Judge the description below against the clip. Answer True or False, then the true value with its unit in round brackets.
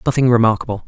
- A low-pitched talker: True (120 Hz)